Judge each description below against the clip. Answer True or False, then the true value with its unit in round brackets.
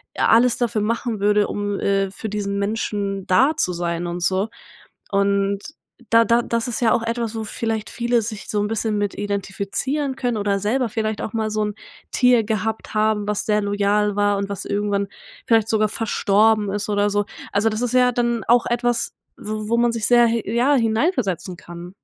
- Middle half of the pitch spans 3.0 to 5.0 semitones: False (2.4 semitones)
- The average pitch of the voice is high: True (215 Hz)